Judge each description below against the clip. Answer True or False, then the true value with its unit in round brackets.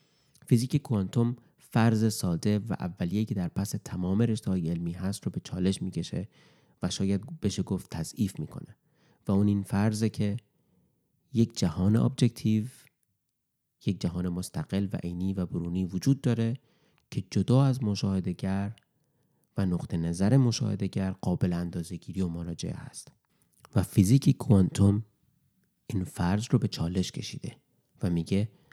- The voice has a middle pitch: False (100 Hz)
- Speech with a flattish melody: False (4.3 semitones)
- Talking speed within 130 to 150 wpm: True (135 wpm)